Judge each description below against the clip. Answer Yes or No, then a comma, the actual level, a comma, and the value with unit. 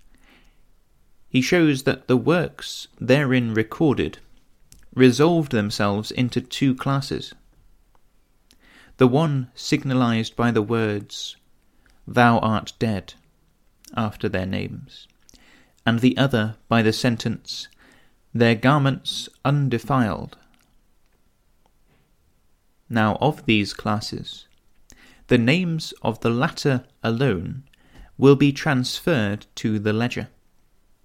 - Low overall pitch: Yes, low, 120 Hz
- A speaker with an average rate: No, slow, 95 wpm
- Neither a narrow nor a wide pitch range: Yes, average, 3.8 semitones